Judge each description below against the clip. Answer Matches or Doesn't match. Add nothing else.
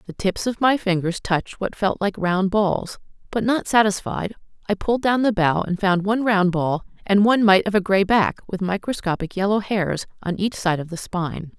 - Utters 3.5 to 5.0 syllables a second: Doesn't match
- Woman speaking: Matches